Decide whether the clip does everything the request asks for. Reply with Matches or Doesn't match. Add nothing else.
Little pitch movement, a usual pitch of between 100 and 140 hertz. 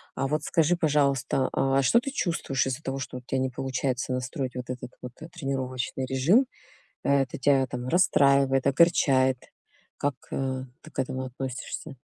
Matches